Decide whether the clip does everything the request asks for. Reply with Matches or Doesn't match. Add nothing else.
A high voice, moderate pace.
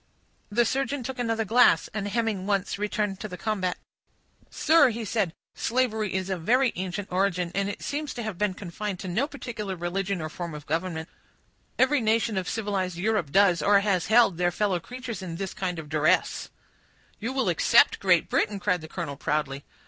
Matches